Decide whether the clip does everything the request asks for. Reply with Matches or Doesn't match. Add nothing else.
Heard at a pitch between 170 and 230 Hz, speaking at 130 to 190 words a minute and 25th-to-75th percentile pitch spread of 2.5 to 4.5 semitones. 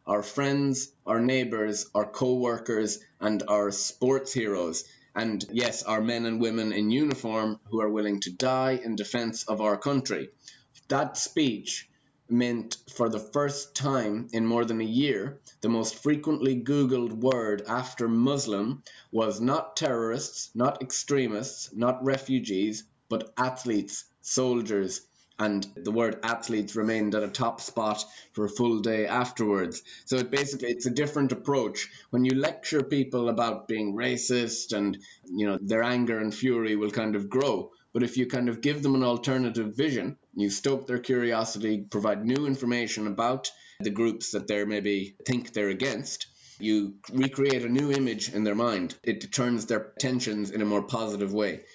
Doesn't match